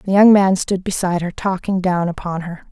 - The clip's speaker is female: Yes, female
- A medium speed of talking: No, fast, 220 wpm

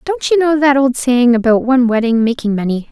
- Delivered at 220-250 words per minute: Yes, fast, 225 wpm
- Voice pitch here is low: No, very high, 255 Hz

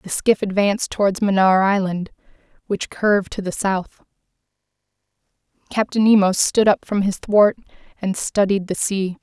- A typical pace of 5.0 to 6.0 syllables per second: No, 4.7 syllables/s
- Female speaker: Yes, female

